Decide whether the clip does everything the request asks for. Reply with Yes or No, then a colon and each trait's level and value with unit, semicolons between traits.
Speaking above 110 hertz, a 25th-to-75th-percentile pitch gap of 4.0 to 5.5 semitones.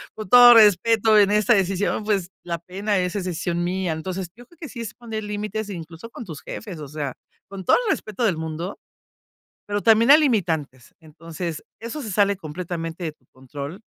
Yes: high, 190 Hz; average, 4.6 semitones